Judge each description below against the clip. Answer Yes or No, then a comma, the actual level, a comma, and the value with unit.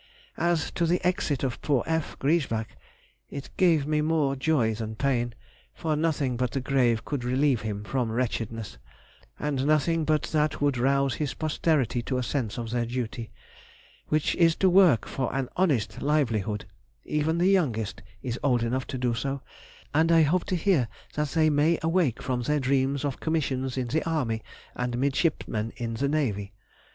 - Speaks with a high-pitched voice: No, low, 135 Hz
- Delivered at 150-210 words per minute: Yes, average, 175 wpm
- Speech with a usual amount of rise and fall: Yes, average, 4.4 semitones